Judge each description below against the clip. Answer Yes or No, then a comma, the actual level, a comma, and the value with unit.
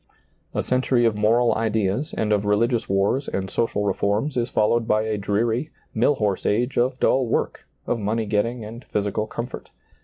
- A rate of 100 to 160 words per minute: No, average, 175 wpm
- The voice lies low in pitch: Yes, low, 110 Hz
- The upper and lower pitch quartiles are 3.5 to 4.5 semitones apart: No, narrow, 2.6 semitones